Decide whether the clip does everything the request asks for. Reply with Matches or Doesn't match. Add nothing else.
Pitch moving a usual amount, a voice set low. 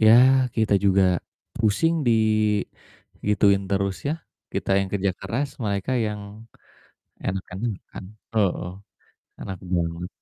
Doesn't match